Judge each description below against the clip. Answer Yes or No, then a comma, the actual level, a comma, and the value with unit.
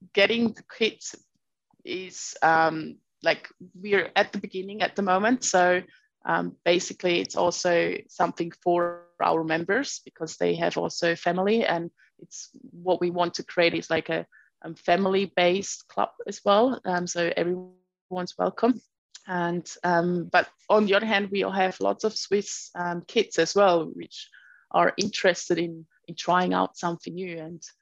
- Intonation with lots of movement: No, average, 2.8 semitones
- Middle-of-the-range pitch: Yes, medium, 180 Hz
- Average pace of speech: Yes, average, 160 wpm